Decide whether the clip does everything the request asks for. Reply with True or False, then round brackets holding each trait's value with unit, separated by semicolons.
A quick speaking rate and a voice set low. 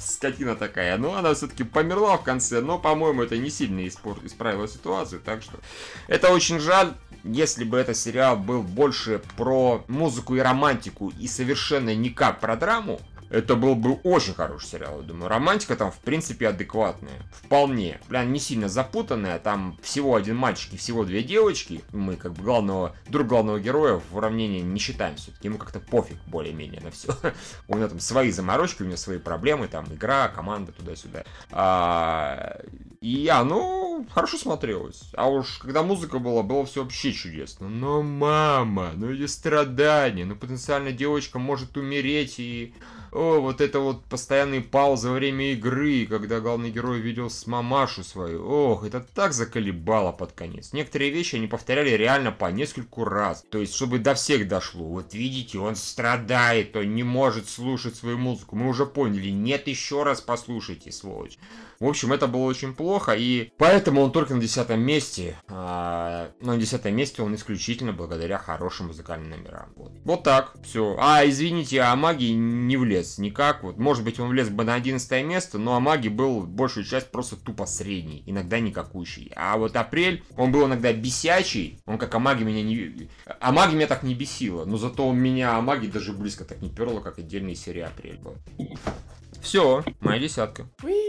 True (170 wpm; 120 Hz)